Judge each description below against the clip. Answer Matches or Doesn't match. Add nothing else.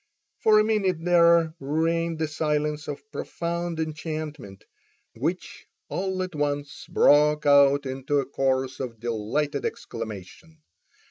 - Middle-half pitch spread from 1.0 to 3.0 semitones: Doesn't match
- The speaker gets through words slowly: Matches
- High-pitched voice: Doesn't match